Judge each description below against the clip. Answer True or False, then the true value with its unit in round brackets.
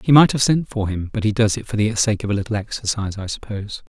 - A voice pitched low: True (105 Hz)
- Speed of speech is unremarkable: False (290 wpm)